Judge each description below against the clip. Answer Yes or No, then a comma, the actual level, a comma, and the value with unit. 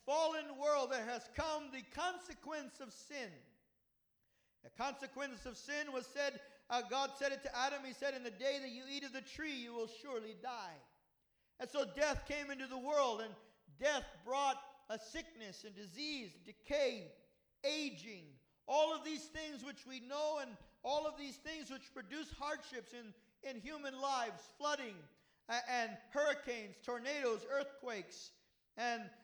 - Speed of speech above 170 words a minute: No, average, 160 wpm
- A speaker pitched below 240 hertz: No, very high, 270 Hz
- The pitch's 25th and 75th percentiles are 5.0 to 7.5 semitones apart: No, average, 3.4 semitones